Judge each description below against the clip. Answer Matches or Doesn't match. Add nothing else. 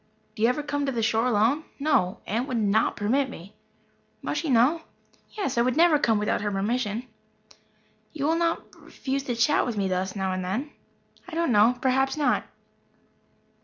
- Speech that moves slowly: Doesn't match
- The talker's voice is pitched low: Doesn't match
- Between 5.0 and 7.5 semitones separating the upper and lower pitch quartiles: Matches